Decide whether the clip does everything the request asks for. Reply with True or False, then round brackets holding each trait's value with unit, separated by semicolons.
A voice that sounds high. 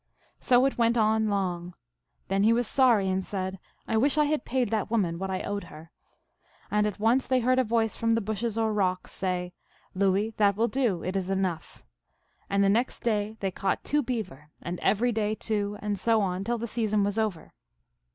True (210 Hz)